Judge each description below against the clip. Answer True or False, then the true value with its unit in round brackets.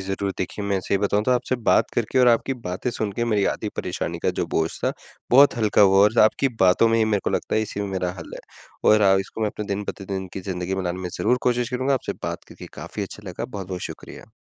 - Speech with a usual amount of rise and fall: True (3.5 semitones)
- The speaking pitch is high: False (100 Hz)